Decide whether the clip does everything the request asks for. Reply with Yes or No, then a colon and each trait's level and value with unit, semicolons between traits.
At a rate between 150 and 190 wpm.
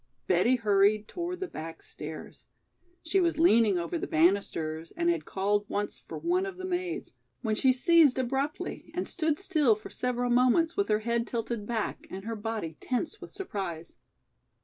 Yes: average, 170 wpm